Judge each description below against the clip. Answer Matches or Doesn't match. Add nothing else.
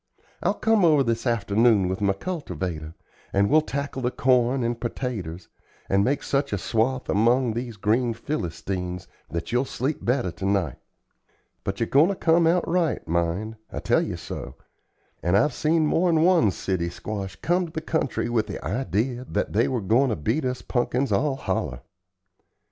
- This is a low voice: Matches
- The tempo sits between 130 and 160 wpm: Doesn't match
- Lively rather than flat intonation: Matches